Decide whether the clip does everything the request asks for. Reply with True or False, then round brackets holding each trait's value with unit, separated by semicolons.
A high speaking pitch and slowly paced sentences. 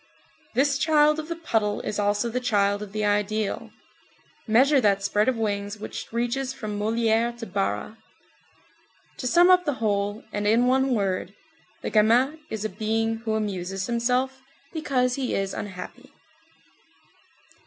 False (225 Hz; 150 wpm)